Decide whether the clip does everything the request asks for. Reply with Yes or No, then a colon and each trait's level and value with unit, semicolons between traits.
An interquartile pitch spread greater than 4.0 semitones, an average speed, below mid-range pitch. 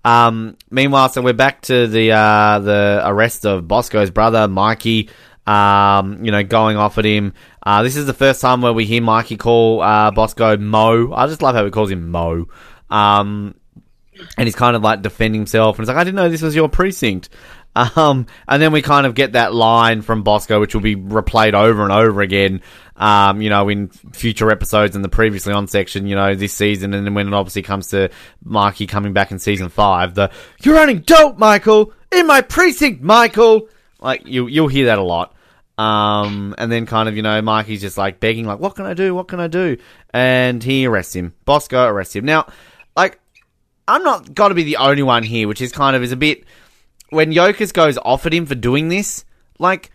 No: average, 4.9 semitones; fast, 215 wpm; low, 110 Hz